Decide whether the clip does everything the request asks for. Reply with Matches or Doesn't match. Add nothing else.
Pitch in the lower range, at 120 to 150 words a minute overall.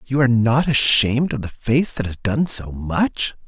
Doesn't match